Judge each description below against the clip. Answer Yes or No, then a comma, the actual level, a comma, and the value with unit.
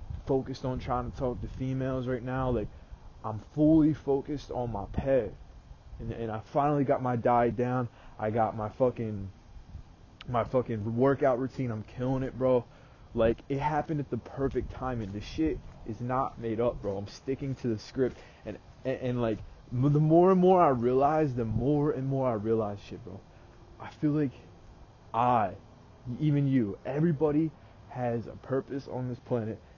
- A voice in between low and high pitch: No, low, 125 Hz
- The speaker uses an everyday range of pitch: Yes, average, 3.3 semitones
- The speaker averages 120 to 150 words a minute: No, average, 175 wpm